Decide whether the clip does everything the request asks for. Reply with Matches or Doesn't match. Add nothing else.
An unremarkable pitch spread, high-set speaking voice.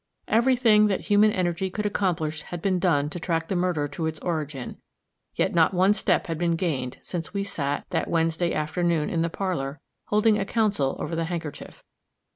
Doesn't match